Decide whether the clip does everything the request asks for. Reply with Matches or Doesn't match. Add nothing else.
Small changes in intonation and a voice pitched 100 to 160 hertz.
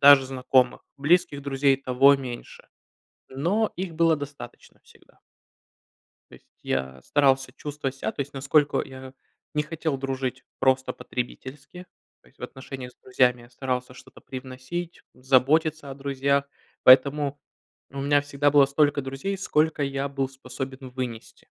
Matches